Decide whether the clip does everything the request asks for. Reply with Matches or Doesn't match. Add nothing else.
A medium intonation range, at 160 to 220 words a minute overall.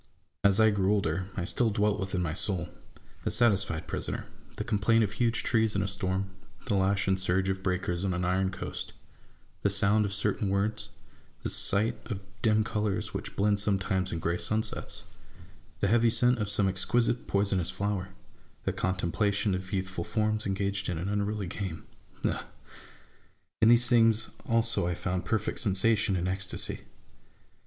Doesn't match